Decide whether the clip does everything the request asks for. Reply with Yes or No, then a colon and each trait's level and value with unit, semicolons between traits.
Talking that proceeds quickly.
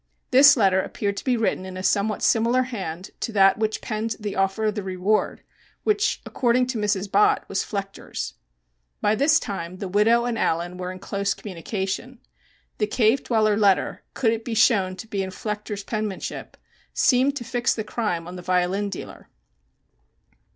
No: average, 175 wpm